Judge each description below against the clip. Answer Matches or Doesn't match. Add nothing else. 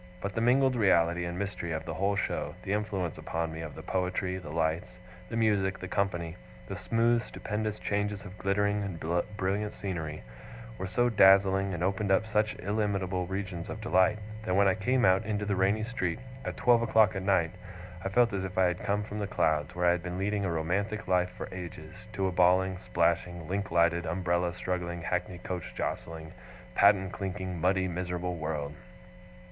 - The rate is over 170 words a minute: Matches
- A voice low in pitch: Matches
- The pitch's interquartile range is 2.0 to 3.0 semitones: Matches